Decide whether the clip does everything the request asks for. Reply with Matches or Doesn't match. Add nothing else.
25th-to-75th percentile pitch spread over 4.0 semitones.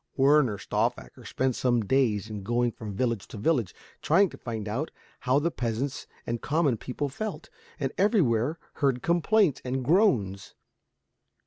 Matches